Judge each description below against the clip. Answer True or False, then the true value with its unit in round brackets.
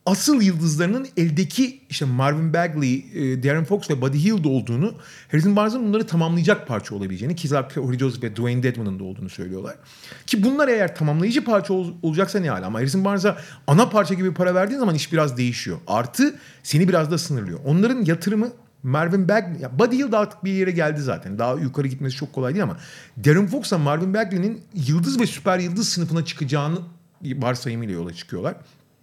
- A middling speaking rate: False (175 wpm)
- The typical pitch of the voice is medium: True (165 Hz)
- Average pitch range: False (6.5 semitones)